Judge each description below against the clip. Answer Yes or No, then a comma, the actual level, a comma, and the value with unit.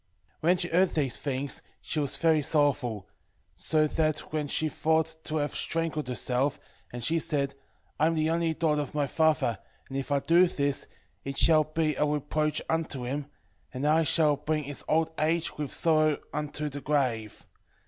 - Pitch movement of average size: No, narrow, 2.1 semitones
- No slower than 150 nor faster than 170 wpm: No, average, 180 wpm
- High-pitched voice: No, medium, 150 Hz